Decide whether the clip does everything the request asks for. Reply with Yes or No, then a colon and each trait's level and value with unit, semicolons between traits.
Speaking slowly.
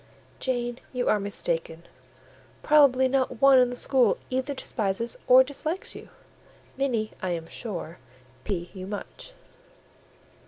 Yes: slow, 125 wpm